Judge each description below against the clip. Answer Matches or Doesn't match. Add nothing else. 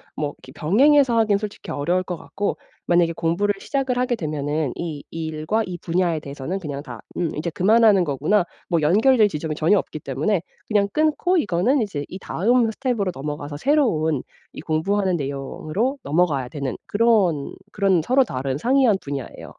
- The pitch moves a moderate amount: Doesn't match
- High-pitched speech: Doesn't match